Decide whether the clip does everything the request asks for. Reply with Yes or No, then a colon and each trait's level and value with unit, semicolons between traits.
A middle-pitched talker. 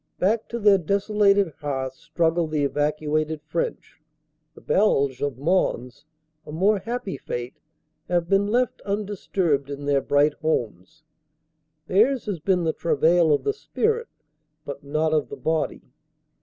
Yes: medium, 160 Hz